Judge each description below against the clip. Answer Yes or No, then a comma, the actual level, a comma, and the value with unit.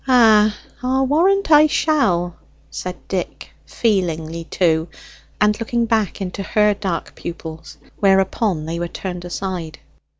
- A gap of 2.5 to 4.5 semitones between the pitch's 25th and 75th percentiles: No, average, 4.9 semitones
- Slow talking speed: Yes, slow, 125 wpm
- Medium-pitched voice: No, high, 195 Hz